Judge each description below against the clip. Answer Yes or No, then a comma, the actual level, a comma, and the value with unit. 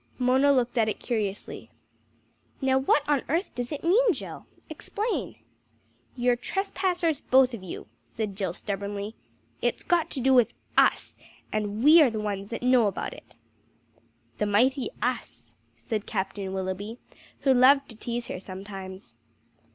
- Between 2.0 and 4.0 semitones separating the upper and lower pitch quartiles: No, average, 5.0 semitones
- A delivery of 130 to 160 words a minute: Yes, average, 150 wpm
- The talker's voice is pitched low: No, high, 240 Hz